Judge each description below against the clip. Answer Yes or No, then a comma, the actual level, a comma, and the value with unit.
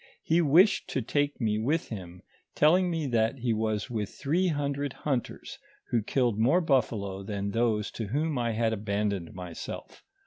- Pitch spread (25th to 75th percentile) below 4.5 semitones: No, wide, 5.4 semitones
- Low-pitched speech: Yes, low, 120 Hz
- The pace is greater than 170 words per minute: No, average, 165 wpm